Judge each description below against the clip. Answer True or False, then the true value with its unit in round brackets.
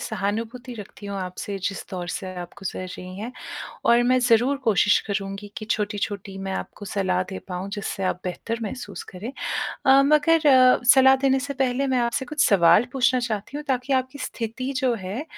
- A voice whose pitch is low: False (225 Hz)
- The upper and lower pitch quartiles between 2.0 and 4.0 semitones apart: False (4.8 semitones)